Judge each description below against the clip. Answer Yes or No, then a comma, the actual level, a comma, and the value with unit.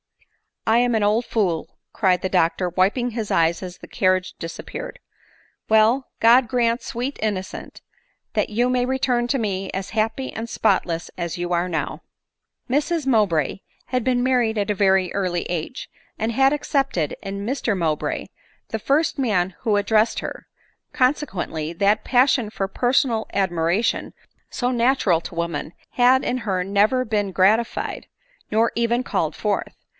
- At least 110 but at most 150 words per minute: No, average, 170 wpm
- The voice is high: Yes, high, 215 Hz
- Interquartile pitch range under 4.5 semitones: No, average, 4.8 semitones